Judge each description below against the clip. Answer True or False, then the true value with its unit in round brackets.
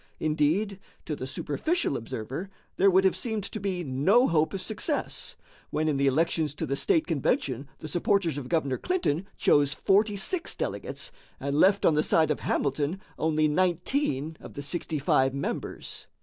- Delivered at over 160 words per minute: True (170 wpm)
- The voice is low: False (160 Hz)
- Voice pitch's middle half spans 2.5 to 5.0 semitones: False (5.4 semitones)